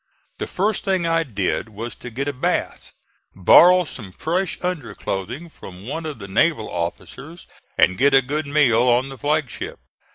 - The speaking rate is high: No, average, 170 wpm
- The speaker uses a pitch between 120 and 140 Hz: Yes, low, 135 Hz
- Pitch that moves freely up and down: Yes, wide, 6.6 semitones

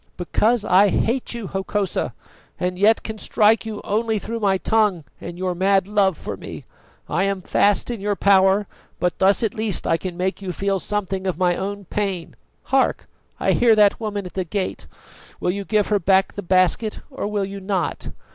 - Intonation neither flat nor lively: No, narrow, 2.0 semitones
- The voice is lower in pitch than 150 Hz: No, high, 200 Hz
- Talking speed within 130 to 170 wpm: No, average, 195 wpm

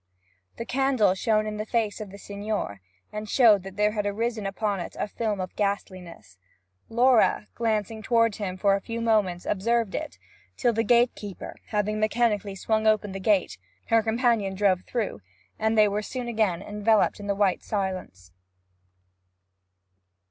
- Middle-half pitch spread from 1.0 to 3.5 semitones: Yes, narrow, 2.4 semitones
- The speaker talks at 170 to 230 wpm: No, average, 160 wpm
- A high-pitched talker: Yes, high, 210 Hz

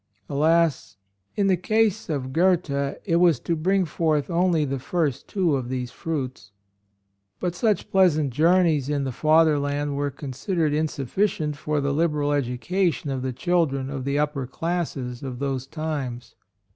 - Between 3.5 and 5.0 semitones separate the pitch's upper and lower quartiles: Yes, average, 3.8 semitones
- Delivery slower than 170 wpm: Yes, average, 155 wpm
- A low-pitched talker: No, medium, 150 Hz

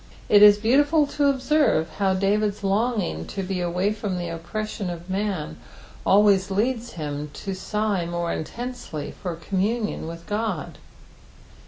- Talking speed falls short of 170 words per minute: Yes, average, 140 wpm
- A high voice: Yes, high, 200 Hz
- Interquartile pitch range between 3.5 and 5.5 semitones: Yes, average, 3.8 semitones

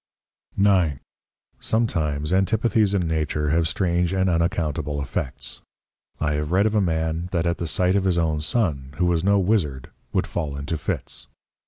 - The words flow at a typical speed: Yes, average, 165 wpm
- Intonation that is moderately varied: Yes, average, 3.8 semitones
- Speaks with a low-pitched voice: Yes, very low, 85 Hz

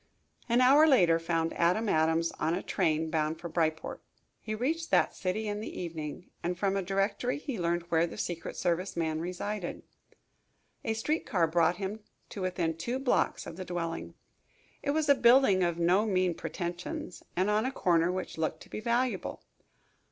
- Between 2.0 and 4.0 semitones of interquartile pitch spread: No, average, 4.5 semitones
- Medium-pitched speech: Yes, medium, 180 Hz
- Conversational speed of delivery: Yes, average, 180 wpm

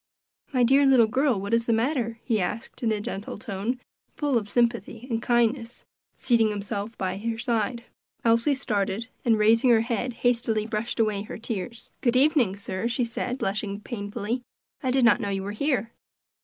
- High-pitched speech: Yes, high, 230 Hz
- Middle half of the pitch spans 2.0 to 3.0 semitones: Yes, narrow, 2.6 semitones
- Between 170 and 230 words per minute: Yes, average, 180 wpm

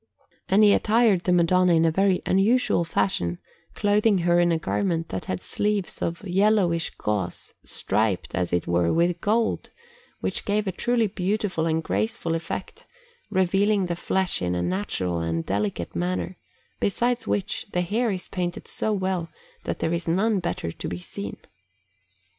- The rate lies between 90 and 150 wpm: No, average, 160 wpm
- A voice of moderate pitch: Yes, medium, 175 Hz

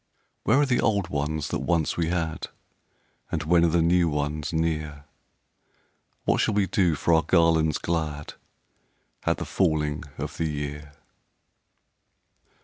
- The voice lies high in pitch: No, very low, 80 Hz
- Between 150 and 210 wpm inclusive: No, average, 140 wpm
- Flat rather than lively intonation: Yes, narrow, 2.3 semitones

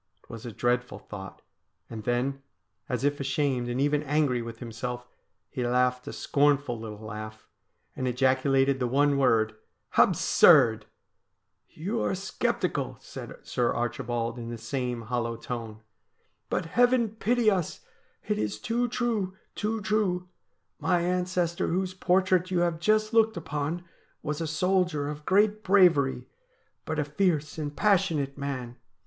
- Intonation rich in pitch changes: Yes, wide, 6.9 semitones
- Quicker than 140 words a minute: Yes, average, 150 wpm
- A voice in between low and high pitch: Yes, medium, 145 Hz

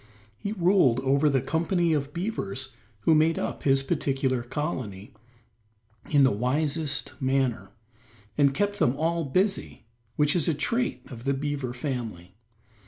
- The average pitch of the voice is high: No, medium, 140 Hz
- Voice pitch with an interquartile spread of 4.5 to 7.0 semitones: No, average, 4.1 semitones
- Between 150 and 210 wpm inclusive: No, average, 140 wpm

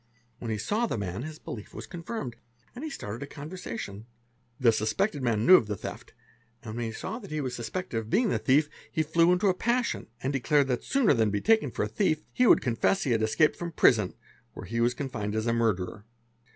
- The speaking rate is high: Yes, fast, 235 wpm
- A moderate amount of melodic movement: No, wide, 8.2 semitones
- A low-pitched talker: Yes, low, 130 Hz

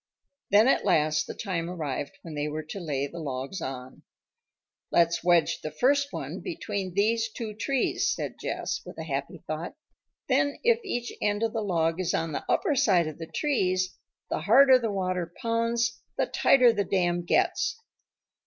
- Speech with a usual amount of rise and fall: No, wide, 6.3 semitones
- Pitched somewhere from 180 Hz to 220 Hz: Yes, medium, 185 Hz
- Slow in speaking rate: No, average, 175 wpm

